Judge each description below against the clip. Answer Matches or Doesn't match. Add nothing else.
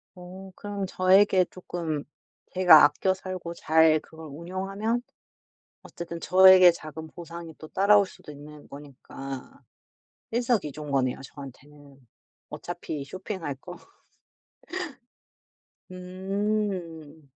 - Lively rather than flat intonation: Doesn't match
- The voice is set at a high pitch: Doesn't match